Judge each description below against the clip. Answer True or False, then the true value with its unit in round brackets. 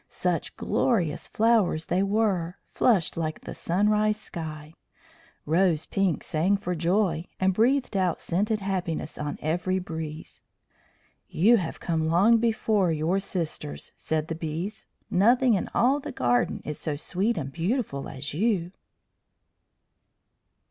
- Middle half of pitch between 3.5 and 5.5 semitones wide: True (4.8 semitones)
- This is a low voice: False (180 Hz)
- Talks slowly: True (130 wpm)